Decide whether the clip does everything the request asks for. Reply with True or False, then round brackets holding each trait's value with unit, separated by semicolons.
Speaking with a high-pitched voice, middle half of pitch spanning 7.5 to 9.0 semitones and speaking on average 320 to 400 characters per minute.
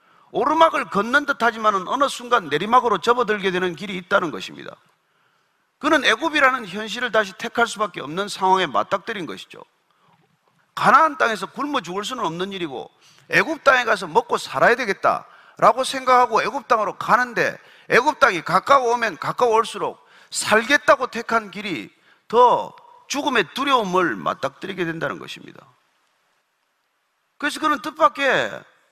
False (240 Hz; 6.2 semitones; 330 characters per minute)